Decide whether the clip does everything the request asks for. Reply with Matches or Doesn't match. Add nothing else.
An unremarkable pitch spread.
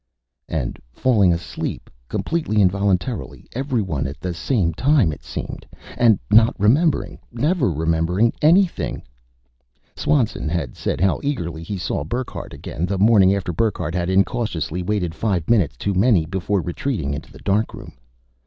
Doesn't match